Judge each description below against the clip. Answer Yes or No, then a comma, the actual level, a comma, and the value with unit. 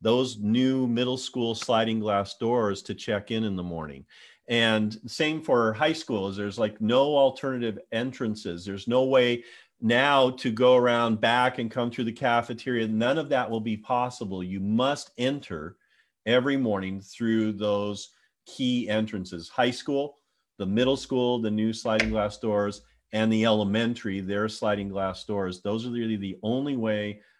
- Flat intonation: No, average, 3.2 semitones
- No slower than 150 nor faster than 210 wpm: Yes, average, 160 wpm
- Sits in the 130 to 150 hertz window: No, low, 115 Hz